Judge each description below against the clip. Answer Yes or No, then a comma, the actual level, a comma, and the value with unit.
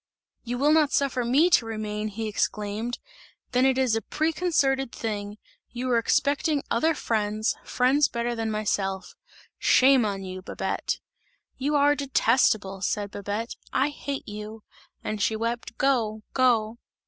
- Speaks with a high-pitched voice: Yes, high, 235 Hz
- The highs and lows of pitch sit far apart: No, average, 4.1 semitones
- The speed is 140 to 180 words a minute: Yes, average, 145 wpm